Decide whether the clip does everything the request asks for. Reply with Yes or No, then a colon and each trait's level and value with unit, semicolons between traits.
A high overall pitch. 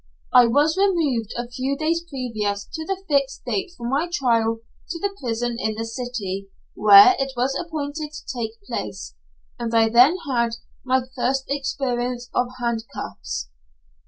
Yes: very high, 250 Hz